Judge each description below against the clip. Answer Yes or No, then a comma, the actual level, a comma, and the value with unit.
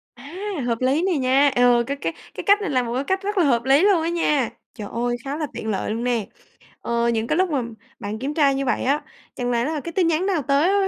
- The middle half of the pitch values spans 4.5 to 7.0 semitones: Yes, wide, 5.5 semitones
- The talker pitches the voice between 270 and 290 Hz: Yes, very high, 275 Hz